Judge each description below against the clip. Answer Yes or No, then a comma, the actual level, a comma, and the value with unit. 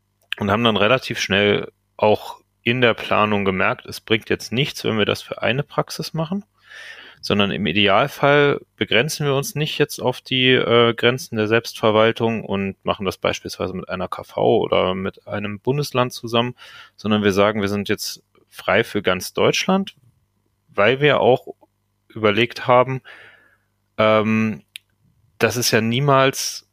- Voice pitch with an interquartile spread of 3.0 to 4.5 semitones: Yes, average, 3.6 semitones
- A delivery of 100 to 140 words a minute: No, average, 150 wpm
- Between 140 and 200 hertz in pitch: No, low, 115 Hz